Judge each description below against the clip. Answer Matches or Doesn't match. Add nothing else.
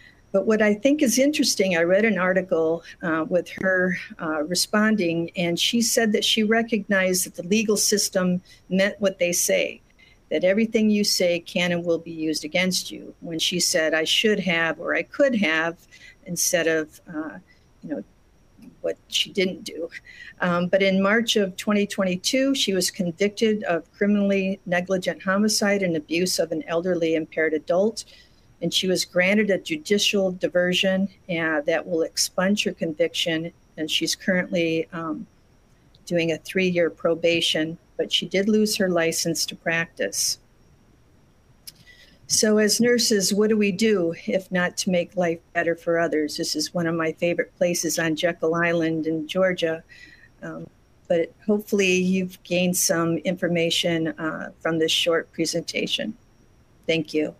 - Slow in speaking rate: Doesn't match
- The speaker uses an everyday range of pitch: Matches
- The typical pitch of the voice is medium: Matches